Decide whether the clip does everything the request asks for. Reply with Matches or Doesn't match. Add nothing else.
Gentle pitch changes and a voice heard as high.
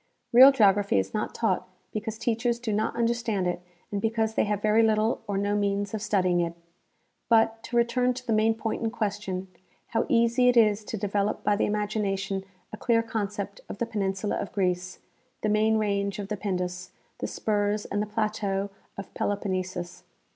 Matches